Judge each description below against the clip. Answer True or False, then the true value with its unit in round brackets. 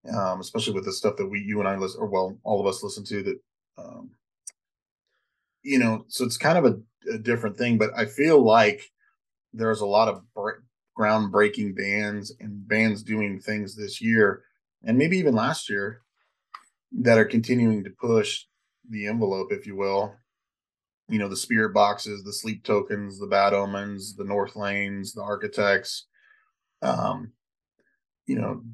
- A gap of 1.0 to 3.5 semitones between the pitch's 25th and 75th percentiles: True (2.4 semitones)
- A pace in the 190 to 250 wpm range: False (170 wpm)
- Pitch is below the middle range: True (105 Hz)